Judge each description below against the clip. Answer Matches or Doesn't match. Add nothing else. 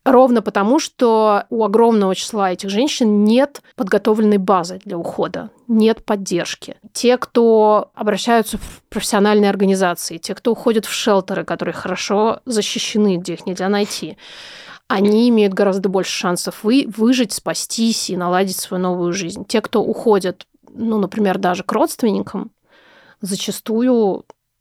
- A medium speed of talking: Matches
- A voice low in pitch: Doesn't match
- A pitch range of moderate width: Matches